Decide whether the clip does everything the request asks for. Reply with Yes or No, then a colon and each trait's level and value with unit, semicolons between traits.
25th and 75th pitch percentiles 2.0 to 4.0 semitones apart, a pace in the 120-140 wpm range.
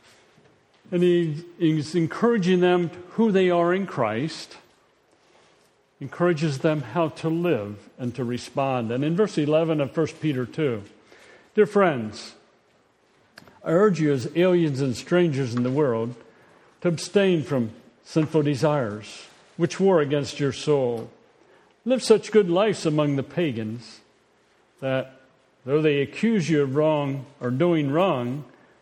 No: average, 5.0 semitones; slow, 135 wpm